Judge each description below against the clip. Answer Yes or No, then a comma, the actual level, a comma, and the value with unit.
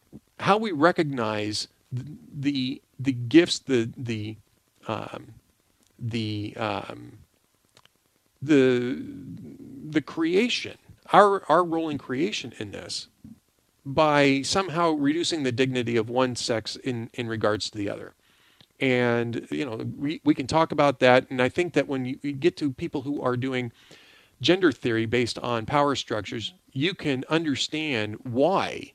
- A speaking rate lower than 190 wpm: Yes, average, 140 wpm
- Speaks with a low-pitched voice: Yes, low, 130 Hz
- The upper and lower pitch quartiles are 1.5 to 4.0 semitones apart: No, average, 4.4 semitones